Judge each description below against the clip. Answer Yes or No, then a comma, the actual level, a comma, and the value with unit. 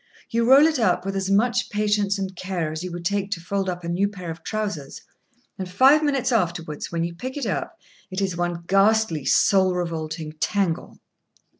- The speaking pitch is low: No, high, 190 Hz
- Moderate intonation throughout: Yes, average, 3.6 semitones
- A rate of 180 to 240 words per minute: Yes, average, 195 wpm